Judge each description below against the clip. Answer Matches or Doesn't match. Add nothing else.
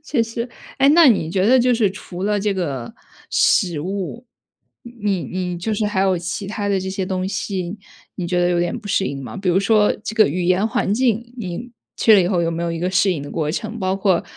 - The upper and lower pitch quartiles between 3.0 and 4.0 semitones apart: Matches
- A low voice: Doesn't match